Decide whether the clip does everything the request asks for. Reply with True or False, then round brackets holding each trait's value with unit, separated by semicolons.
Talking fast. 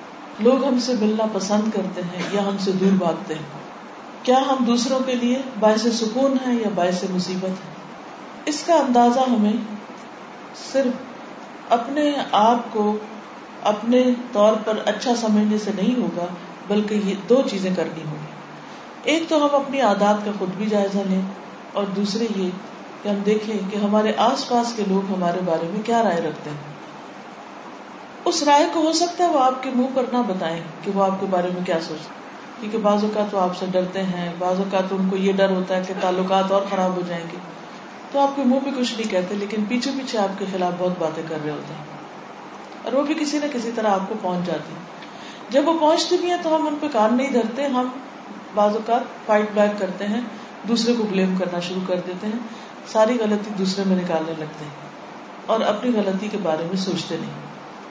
True (195 wpm)